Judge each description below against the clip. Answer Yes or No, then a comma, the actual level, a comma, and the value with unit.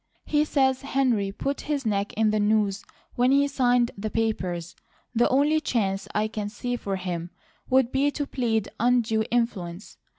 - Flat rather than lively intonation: No, average, 4.4 semitones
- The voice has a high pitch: Yes, high, 225 Hz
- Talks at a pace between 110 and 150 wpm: No, average, 165 wpm